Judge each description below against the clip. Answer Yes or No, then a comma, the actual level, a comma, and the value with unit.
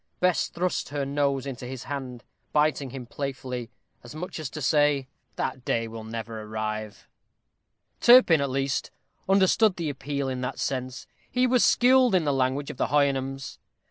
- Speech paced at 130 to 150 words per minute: No, average, 165 wpm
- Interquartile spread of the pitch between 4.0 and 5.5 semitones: No, average, 3.4 semitones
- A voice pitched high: No, low, 135 Hz